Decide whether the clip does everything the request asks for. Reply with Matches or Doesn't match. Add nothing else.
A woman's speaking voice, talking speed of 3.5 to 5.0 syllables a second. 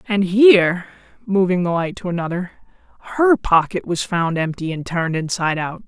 Doesn't match